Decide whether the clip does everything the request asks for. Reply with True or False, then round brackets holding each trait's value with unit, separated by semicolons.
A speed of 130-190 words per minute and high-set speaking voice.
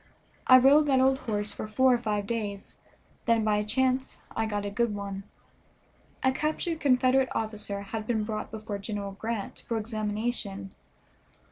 True (160 wpm; 220 Hz)